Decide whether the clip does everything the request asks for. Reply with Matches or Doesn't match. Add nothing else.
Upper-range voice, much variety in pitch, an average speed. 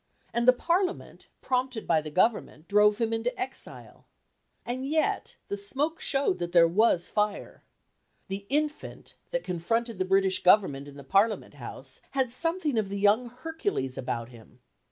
Matches